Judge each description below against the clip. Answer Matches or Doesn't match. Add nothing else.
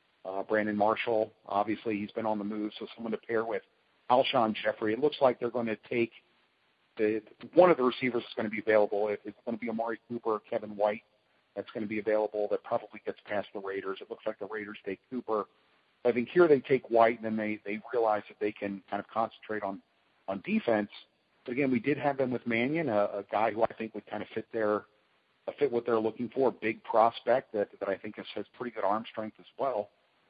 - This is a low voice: Matches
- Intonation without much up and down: Matches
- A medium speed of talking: Doesn't match